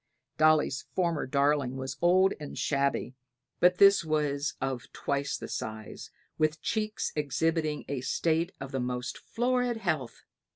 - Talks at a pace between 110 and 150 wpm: Yes, average, 140 wpm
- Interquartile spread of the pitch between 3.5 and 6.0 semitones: Yes, average, 4.2 semitones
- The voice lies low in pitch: No, medium, 150 Hz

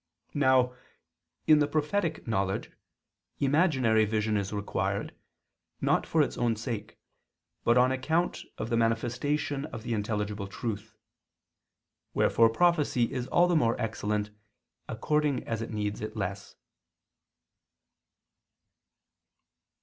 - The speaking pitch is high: No, low, 115 Hz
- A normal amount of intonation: Yes, average, 5.0 semitones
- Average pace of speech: No, slow, 110 wpm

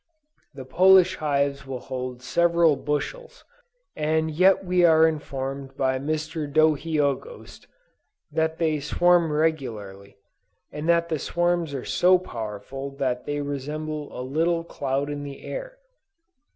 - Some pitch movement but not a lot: Yes, average, 3.5 semitones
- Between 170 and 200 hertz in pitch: No, medium, 150 Hz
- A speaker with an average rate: No, slow, 125 wpm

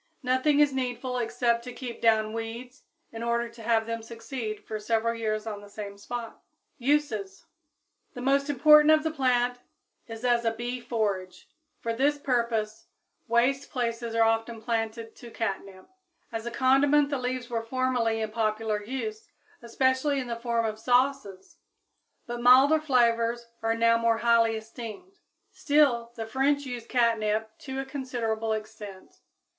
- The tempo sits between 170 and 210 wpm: No, average, 155 wpm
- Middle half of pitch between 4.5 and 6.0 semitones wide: No, narrow, 2.5 semitones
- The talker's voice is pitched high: Yes, high, 235 Hz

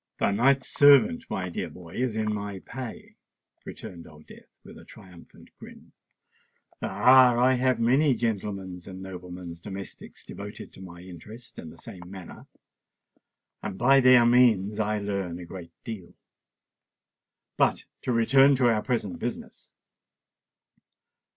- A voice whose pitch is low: Yes, low, 105 Hz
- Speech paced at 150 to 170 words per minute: No, average, 140 wpm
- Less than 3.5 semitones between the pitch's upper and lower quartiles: No, average, 5.2 semitones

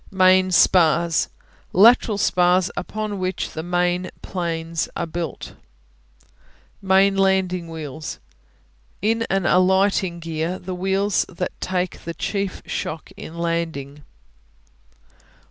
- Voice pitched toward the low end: No, medium, 180 Hz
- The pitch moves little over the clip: Yes, narrow, 2.3 semitones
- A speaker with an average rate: No, slow, 105 wpm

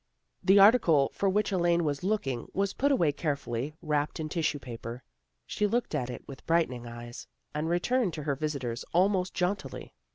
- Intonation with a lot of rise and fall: Yes, wide, 5.9 semitones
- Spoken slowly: No, average, 170 wpm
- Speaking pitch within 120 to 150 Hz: No, medium, 160 Hz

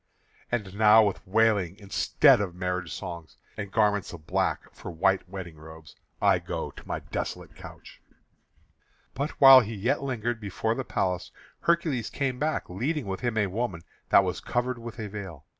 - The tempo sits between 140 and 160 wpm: No, average, 170 wpm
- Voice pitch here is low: Yes, low, 105 Hz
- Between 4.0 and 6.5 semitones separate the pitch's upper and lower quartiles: Yes, average, 4.8 semitones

